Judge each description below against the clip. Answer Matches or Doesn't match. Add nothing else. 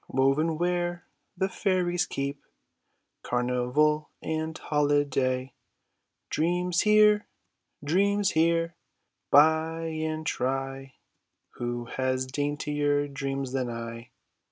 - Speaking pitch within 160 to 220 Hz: Doesn't match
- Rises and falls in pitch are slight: Doesn't match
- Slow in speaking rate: Matches